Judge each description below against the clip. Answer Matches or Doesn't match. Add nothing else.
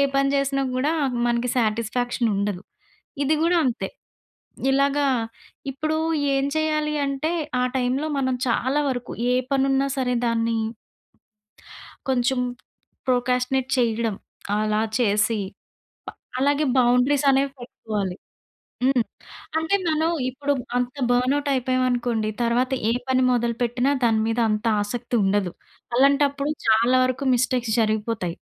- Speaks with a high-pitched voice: Matches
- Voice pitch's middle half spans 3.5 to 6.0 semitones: Doesn't match